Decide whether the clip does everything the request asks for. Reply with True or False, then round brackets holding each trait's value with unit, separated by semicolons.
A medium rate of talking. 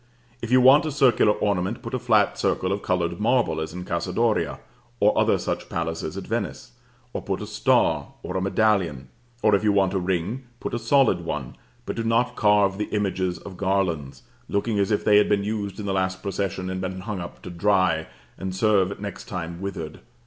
False (210 wpm)